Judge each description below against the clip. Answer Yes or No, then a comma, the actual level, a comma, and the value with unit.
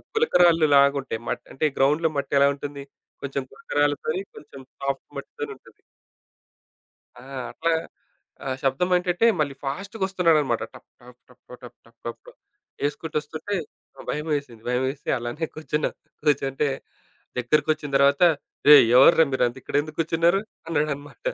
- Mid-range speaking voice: Yes, medium, 145 Hz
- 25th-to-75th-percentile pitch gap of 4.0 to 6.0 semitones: No, average, 3.1 semitones